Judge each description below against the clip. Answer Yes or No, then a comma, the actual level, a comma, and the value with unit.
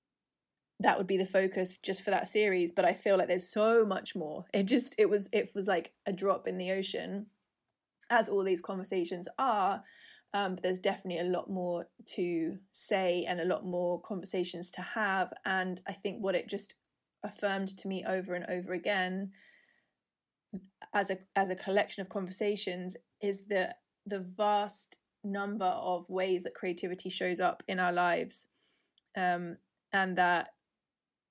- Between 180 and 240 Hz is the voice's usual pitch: Yes, high, 190 Hz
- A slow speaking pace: No, average, 165 wpm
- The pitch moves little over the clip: Yes, narrow, 1.9 semitones